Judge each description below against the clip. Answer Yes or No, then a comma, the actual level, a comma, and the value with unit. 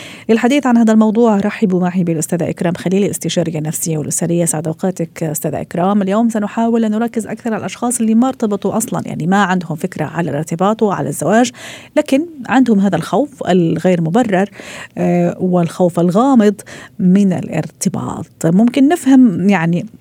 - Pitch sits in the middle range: No, high, 195 Hz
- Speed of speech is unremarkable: No, fast, 140 wpm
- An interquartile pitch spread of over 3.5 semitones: Yes, average, 4.7 semitones